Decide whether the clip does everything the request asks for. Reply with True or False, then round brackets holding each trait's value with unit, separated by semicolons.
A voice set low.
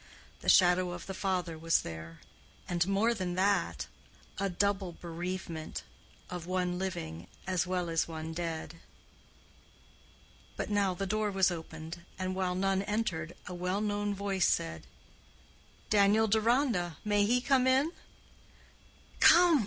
False (185 Hz)